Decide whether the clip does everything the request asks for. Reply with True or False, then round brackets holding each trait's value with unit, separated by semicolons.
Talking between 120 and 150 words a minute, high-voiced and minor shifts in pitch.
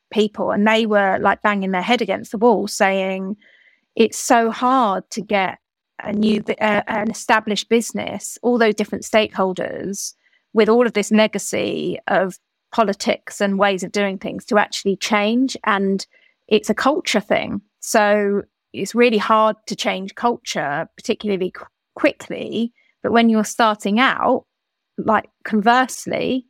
True (145 wpm; 215 Hz; 2.3 semitones)